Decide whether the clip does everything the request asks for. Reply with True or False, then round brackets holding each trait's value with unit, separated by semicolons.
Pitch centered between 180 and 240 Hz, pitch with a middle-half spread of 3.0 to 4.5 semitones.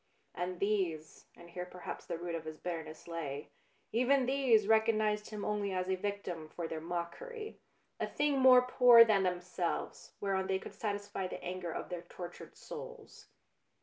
True (190 Hz; 4.1 semitones)